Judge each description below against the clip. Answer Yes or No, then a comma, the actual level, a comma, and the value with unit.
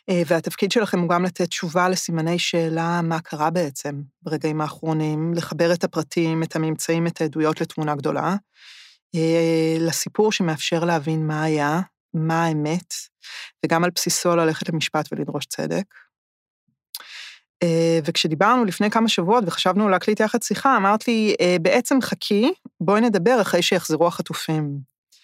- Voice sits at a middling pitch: Yes, medium, 170 Hz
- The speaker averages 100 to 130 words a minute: Yes, average, 125 wpm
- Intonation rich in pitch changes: No, average, 2.9 semitones